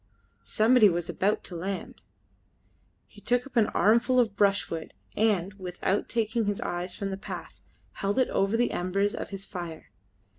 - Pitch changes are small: No, average, 3.4 semitones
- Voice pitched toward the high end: Yes, high, 200 Hz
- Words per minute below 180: Yes, average, 160 wpm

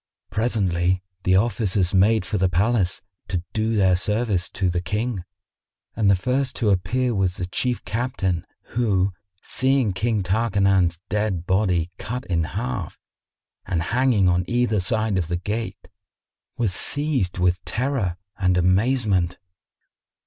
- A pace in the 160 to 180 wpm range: No, slow, 135 wpm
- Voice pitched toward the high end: No, low, 100 Hz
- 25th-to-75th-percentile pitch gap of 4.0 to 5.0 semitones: Yes, average, 4.3 semitones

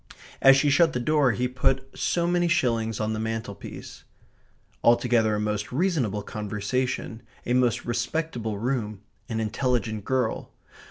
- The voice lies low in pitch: Yes, low, 120 Hz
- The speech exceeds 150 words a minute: No, average, 140 wpm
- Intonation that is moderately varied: Yes, average, 3.5 semitones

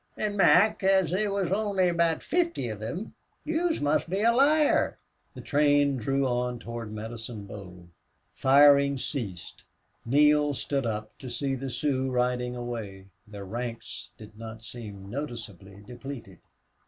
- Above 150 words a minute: No, average, 140 wpm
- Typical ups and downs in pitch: No, wide, 6.4 semitones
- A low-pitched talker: Yes, low, 130 Hz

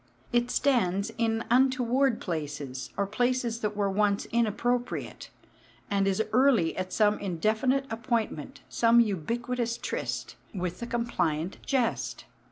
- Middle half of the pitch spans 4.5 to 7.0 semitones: No, average, 3.9 semitones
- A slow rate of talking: Yes, slow, 120 wpm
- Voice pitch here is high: Yes, high, 225 Hz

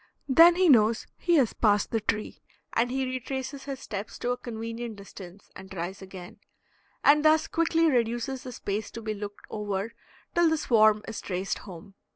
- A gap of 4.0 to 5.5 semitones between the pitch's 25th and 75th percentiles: Yes, average, 4.7 semitones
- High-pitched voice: Yes, high, 230 Hz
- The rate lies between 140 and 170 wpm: No, average, 180 wpm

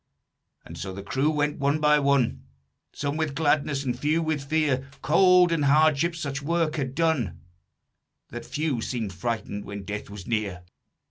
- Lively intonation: No, average, 4.7 semitones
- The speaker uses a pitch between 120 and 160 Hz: Yes, medium, 140 Hz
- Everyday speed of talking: Yes, average, 160 wpm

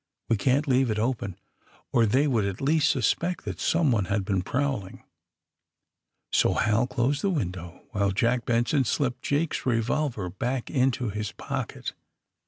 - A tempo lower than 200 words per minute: Yes, average, 155 wpm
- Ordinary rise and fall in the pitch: Yes, average, 4.5 semitones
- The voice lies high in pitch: No, low, 120 Hz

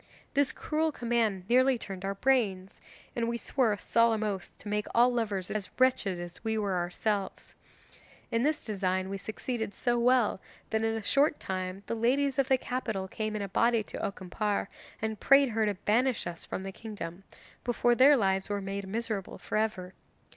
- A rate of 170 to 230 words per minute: Yes, average, 185 wpm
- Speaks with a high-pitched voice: Yes, high, 215 Hz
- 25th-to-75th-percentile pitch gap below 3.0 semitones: No, average, 3.8 semitones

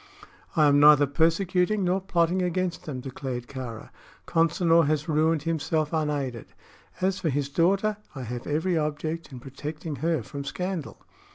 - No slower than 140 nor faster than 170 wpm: Yes, average, 150 wpm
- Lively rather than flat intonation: No, average, 3.3 semitones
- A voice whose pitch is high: No, medium, 155 Hz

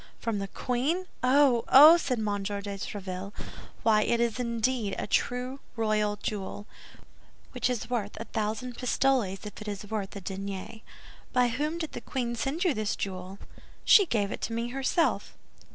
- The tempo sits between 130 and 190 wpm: Yes, average, 170 wpm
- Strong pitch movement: No, average, 3.8 semitones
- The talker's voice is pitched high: Yes, high, 230 Hz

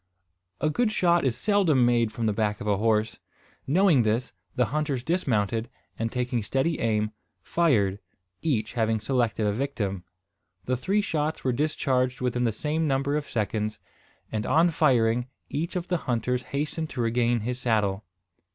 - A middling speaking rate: Yes, average, 160 wpm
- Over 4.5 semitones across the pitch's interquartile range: Yes, average, 5.2 semitones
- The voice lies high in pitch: No, low, 125 Hz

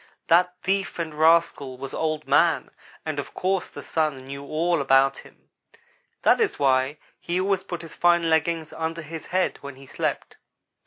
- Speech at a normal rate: Yes, average, 170 wpm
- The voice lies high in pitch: No, medium, 160 Hz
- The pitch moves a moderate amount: Yes, average, 3.7 semitones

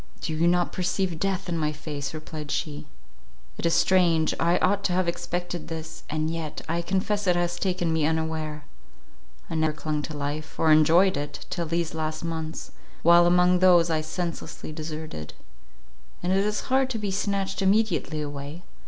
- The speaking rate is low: No, average, 175 wpm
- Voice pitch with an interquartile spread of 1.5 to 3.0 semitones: Yes, narrow, 2.6 semitones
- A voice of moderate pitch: Yes, medium, 165 Hz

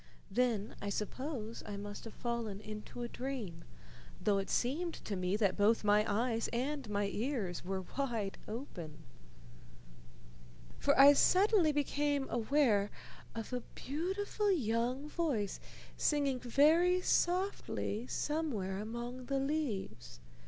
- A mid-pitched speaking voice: No, high, 240 Hz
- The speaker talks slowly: Yes, slow, 125 wpm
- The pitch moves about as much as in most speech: No, wide, 5.8 semitones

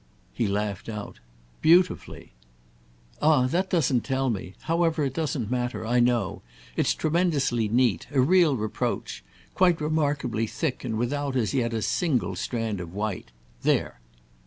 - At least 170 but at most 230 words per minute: No, slow, 135 wpm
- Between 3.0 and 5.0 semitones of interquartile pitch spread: No, wide, 5.5 semitones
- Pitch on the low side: Yes, low, 125 Hz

